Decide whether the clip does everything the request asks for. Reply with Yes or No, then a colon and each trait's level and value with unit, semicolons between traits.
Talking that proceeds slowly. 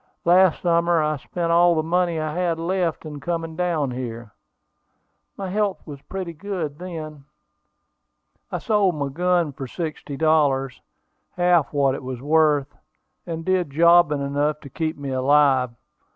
No: average, 150 wpm